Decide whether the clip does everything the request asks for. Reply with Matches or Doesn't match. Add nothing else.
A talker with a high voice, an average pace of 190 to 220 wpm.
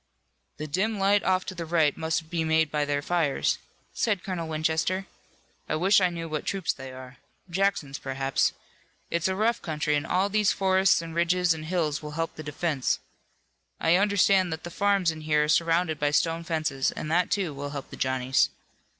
Doesn't match